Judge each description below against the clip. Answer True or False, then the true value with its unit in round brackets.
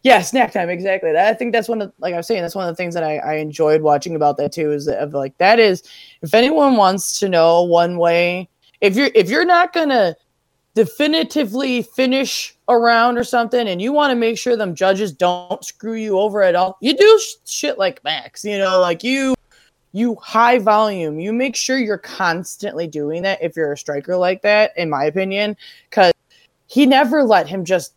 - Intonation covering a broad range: True (6.1 semitones)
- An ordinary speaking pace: False (210 wpm)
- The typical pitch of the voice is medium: False (205 Hz)